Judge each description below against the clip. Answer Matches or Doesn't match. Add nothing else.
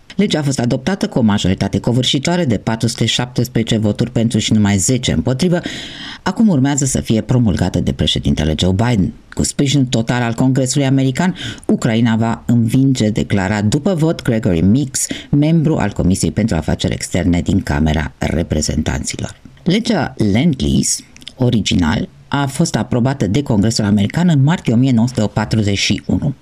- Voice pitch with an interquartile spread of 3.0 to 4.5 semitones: Doesn't match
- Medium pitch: Doesn't match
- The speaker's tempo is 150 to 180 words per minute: Doesn't match